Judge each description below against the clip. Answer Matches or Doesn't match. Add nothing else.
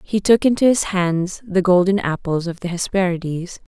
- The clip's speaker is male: Doesn't match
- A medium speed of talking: Matches